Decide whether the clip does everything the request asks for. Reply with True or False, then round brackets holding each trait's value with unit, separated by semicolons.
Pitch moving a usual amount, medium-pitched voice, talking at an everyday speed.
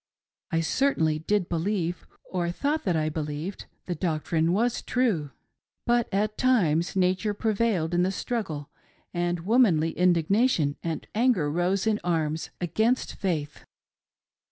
False (4.9 semitones; 180 Hz; 130 wpm)